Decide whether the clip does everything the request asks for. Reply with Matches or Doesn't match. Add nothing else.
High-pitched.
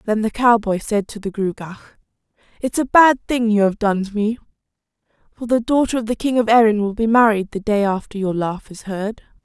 Matches